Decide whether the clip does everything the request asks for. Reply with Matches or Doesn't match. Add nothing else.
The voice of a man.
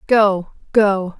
Doesn't match